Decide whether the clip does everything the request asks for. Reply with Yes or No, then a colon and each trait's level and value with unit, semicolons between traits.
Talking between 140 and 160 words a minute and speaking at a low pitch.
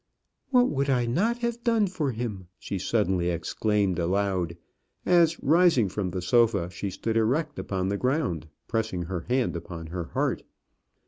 Yes: average, 155 wpm; low, 110 Hz